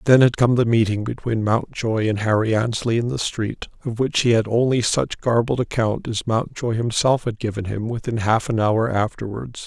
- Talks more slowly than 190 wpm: No, average, 200 wpm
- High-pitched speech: No, low, 115 Hz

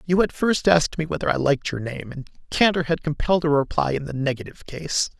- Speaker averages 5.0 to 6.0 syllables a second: No, 6.2 syllables/s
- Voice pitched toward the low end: No, medium, 150 Hz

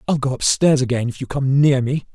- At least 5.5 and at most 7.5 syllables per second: Yes, 5.7 syllables/s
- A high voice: No, low, 135 Hz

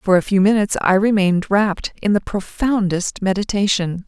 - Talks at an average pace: Yes, average, 160 wpm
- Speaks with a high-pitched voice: Yes, high, 200 Hz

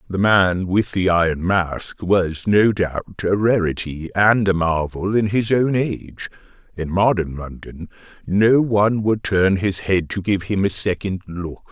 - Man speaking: Yes, male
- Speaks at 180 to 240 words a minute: No, average, 170 wpm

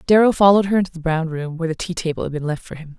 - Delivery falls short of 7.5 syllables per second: No, 7.7 syllables/s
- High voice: No, medium, 170 Hz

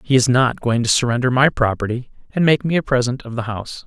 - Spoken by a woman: No, male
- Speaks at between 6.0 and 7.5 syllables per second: Yes, 6.1 syllables/s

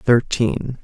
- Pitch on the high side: No, low, 120 Hz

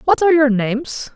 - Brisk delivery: Yes, fast, 210 wpm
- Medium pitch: No, very high, 270 Hz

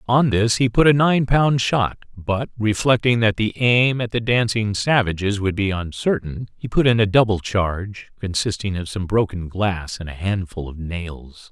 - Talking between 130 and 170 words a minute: No, average, 190 wpm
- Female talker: No, male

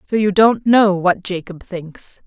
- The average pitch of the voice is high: Yes, high, 195 Hz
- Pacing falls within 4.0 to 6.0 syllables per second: No, 3.8 syllables/s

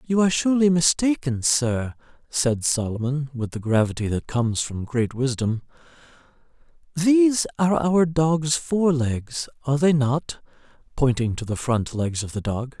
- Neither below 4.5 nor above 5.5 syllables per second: Yes, 4.6 syllables/s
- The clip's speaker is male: Yes, male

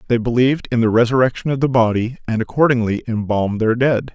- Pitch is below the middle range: Yes, low, 120 Hz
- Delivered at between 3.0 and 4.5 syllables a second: No, 6.4 syllables/s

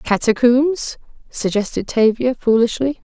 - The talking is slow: Yes, slow, 75 wpm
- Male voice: No, female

